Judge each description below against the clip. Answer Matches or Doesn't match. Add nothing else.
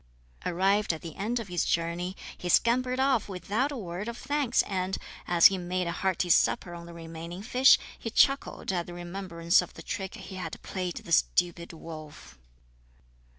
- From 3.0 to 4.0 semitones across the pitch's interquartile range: Matches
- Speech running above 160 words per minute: Matches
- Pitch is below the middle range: Doesn't match